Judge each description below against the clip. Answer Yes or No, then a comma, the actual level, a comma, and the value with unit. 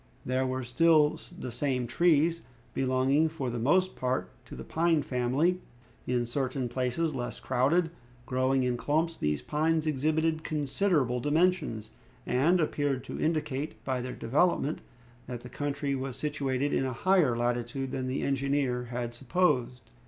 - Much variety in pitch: No, average, 3.9 semitones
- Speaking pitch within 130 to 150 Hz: Yes, low, 135 Hz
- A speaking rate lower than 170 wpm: Yes, average, 145 wpm